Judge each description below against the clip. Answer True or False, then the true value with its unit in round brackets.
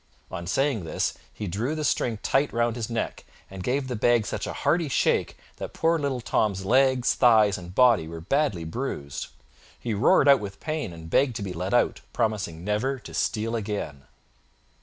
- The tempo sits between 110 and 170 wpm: False (185 wpm)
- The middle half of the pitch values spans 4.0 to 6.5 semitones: True (5.4 semitones)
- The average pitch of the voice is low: True (115 Hz)